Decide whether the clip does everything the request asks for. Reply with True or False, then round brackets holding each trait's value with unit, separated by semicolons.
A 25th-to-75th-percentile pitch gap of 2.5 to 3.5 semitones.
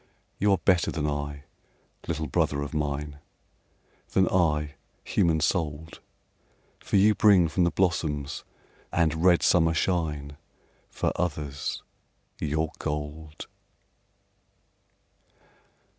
True (2.9 semitones)